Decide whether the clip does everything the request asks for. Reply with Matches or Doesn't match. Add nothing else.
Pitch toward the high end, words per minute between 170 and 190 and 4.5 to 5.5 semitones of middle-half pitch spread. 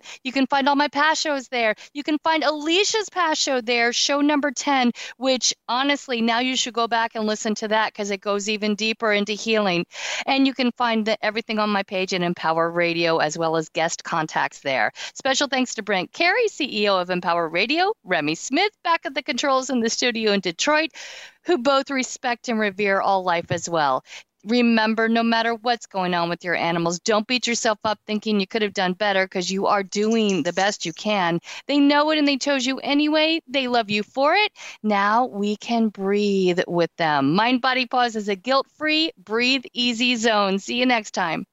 Doesn't match